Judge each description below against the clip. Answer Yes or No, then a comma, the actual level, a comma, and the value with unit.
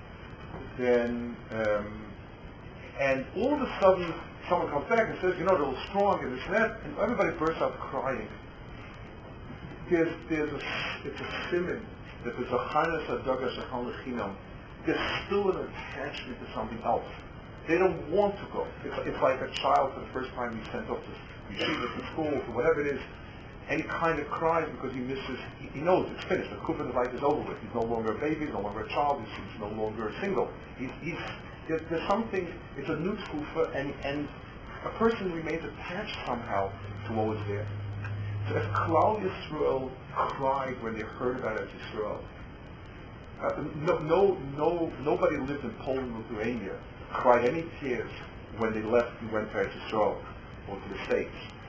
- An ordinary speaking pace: Yes, average, 175 wpm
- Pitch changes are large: Yes, wide, 6.4 semitones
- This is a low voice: Yes, low, 130 Hz